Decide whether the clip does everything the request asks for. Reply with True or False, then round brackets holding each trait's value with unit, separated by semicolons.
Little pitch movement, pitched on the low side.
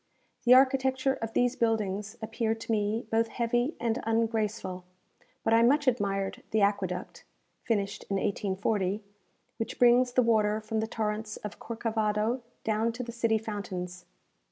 False (2.1 semitones; 225 Hz)